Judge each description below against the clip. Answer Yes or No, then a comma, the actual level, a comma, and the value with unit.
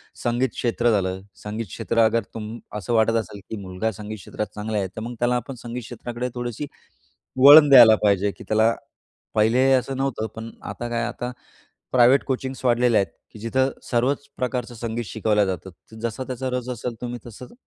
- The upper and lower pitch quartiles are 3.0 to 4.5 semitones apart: No, narrow, 2.4 semitones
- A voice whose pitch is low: Yes, low, 120 Hz